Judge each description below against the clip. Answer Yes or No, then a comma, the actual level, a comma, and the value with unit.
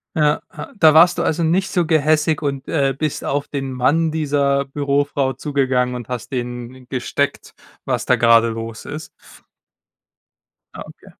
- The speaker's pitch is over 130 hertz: Yes, medium, 140 Hz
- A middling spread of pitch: Yes, average, 3.5 semitones